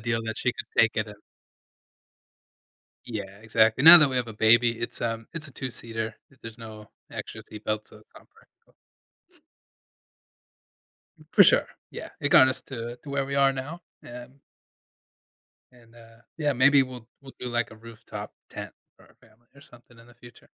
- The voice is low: Yes, low, 120 Hz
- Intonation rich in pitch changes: No, average, 2.7 semitones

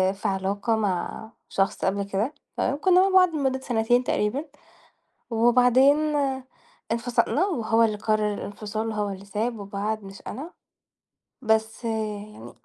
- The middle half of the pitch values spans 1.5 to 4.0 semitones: Yes, average, 3.2 semitones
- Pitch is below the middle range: No, high, 220 Hz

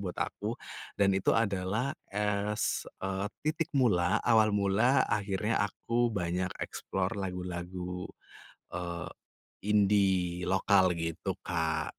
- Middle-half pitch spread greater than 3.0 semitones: No, average, 2.7 semitones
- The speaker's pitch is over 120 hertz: No, very low, 95 Hz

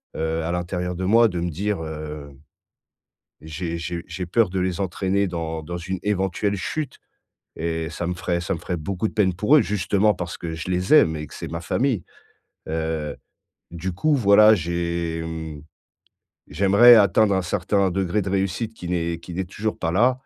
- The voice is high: No, very low, 90 Hz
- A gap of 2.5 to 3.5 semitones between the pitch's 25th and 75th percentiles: Yes, average, 3.2 semitones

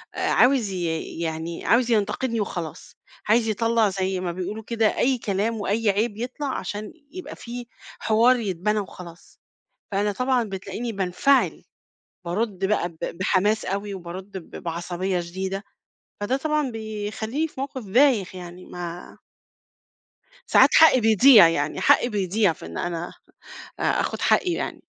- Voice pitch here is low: No, high, 205 Hz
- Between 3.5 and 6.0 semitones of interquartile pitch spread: Yes, average, 4.2 semitones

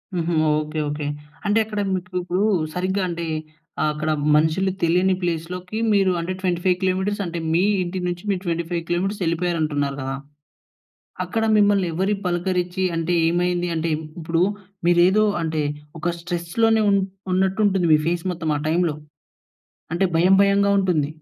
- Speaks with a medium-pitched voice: Yes, medium, 175 Hz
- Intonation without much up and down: Yes, narrow, 2.2 semitones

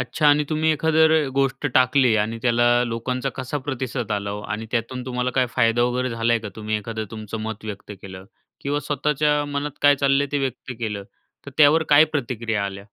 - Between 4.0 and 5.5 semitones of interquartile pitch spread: Yes, average, 4.3 semitones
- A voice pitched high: No, low, 125 Hz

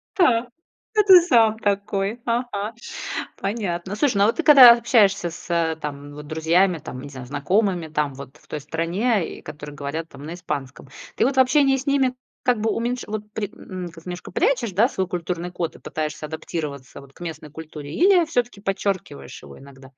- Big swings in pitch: Yes, wide, 7.4 semitones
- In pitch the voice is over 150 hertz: Yes, medium, 185 Hz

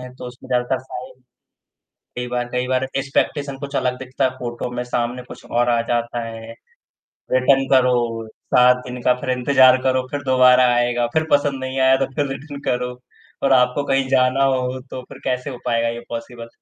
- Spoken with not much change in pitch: Yes, narrow, 1.4 semitones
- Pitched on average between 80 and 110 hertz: No, low, 125 Hz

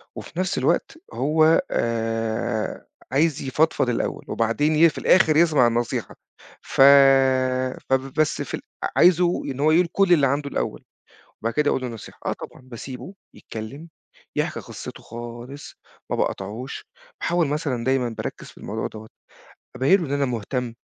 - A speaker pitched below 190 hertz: Yes, low, 135 Hz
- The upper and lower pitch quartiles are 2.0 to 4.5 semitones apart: No, average, 4.9 semitones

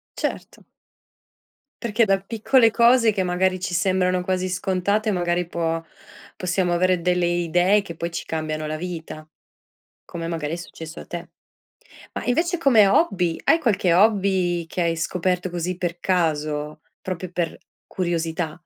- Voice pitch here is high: No, medium, 180 Hz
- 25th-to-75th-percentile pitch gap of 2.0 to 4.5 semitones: Yes, narrow, 2.4 semitones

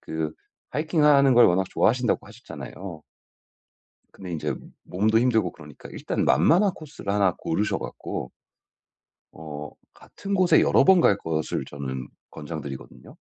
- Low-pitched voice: Yes, very low, 95 Hz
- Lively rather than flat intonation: Yes, wide, 8.8 semitones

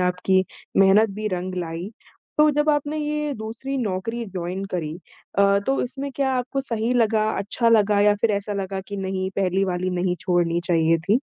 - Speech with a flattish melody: No, average, 4.5 semitones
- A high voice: Yes, high, 200 Hz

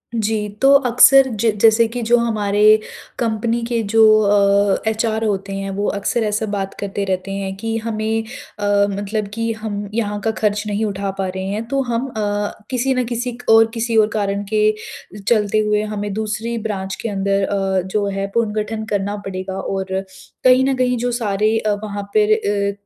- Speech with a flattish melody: Yes, narrow, 2.1 semitones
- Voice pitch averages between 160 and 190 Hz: No, high, 210 Hz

